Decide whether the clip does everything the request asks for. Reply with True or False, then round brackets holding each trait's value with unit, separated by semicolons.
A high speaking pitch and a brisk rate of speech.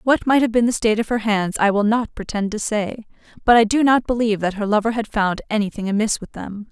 True (220 Hz; 260 wpm)